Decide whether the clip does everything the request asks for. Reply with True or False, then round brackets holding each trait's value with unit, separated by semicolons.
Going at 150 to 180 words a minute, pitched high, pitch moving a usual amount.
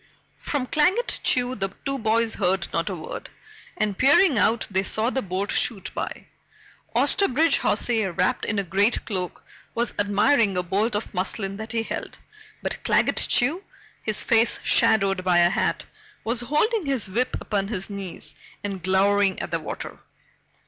True (165 wpm; 210 Hz; 4.2 semitones)